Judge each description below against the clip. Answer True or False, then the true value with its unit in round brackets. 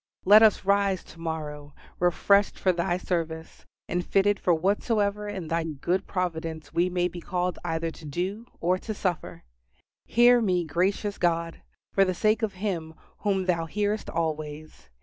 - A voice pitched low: False (180 Hz)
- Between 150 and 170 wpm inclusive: True (160 wpm)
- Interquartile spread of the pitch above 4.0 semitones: False (3.5 semitones)